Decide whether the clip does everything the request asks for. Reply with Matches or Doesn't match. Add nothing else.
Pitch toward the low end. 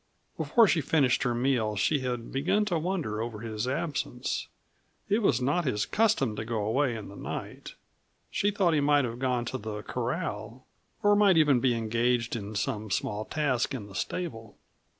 Matches